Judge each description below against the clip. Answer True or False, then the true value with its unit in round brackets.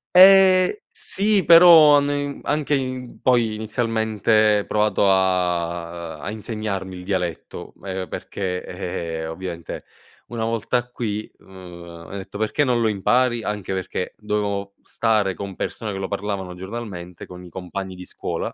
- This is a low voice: True (105 Hz)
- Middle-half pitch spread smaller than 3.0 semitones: False (4.3 semitones)